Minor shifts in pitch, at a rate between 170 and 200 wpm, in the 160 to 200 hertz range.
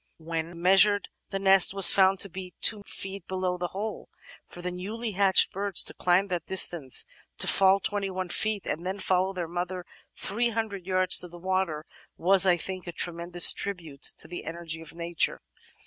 Yes: narrow, 2.0 semitones; average, 180 wpm; medium, 185 Hz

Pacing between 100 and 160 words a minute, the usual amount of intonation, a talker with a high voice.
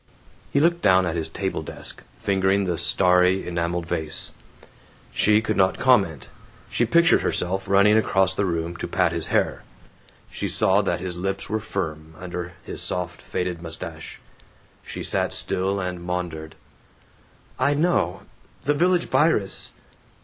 No: average, 145 wpm; average, 3.2 semitones; very low, 95 Hz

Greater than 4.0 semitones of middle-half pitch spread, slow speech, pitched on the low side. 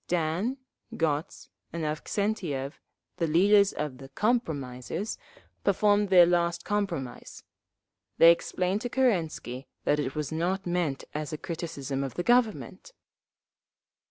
No: average, 5.1 semitones; slow, 120 wpm; medium, 170 Hz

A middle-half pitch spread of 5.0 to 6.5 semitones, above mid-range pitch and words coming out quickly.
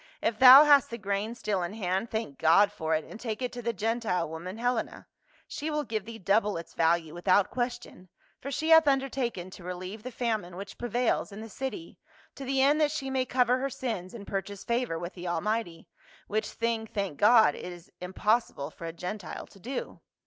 Yes: average, 5.3 semitones; high, 220 Hz; fast, 215 wpm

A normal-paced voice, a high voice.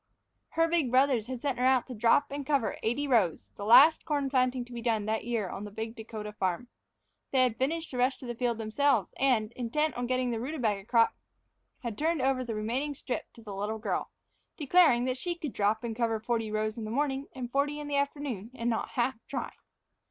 No: fast, 225 wpm; high, 245 Hz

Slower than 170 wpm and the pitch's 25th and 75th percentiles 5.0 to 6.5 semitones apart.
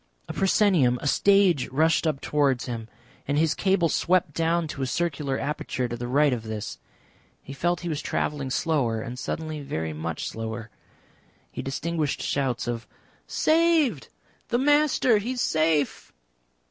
Yes: average, 155 wpm; wide, 5.5 semitones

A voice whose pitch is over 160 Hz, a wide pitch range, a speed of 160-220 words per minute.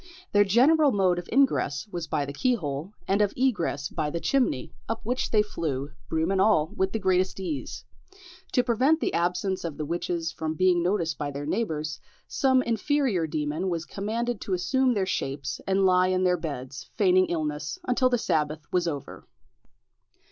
Yes: medium, 185 Hz; wide, 5.8 semitones; average, 175 wpm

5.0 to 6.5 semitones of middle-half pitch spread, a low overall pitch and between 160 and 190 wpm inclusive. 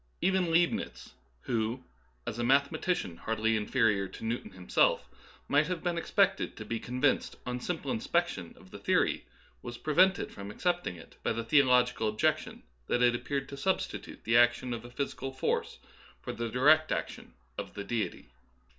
Yes: wide, 5.6 semitones; low, 125 Hz; average, 170 wpm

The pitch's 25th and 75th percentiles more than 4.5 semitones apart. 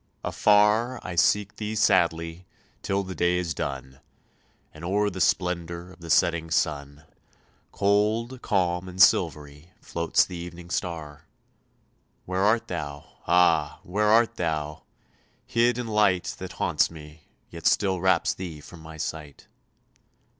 No: average, 3.8 semitones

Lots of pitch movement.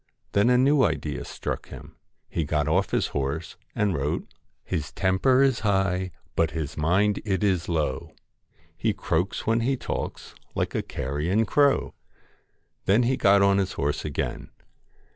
Yes: wide, 5.8 semitones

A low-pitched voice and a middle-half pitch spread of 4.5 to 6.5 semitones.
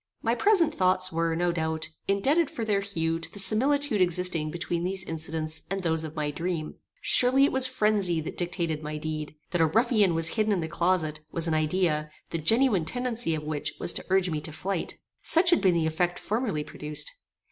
No: medium, 175 Hz; average, 4.8 semitones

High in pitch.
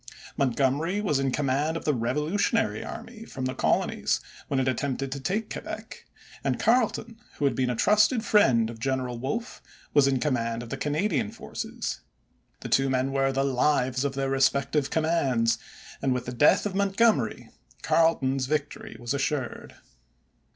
No: low, 135 Hz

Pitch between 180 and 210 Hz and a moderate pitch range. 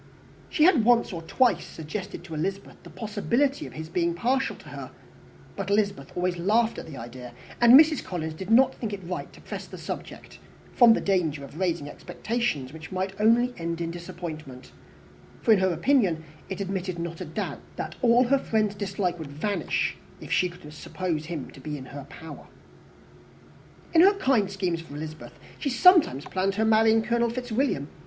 No: high, 190 Hz; wide, 5.9 semitones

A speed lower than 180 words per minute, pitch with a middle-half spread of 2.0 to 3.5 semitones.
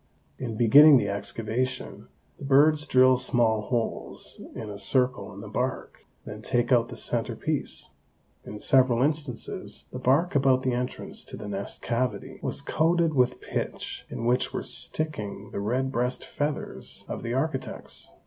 Yes: average, 160 wpm; average, 2.8 semitones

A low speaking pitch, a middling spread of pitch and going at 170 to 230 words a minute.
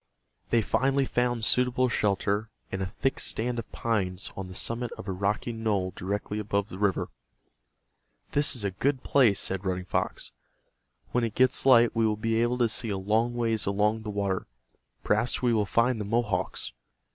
Yes: low, 110 Hz; average, 3.2 semitones; average, 180 wpm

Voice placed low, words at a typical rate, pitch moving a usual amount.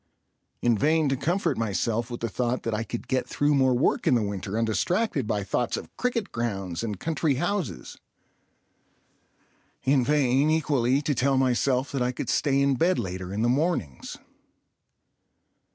Yes: low, 125 Hz; average, 165 wpm; average, 4.3 semitones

